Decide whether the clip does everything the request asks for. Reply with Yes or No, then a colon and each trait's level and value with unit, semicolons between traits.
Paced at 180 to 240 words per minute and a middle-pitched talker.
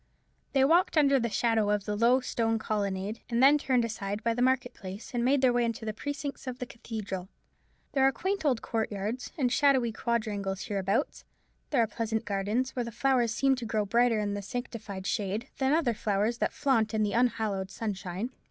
No: average, 200 wpm; high, 230 Hz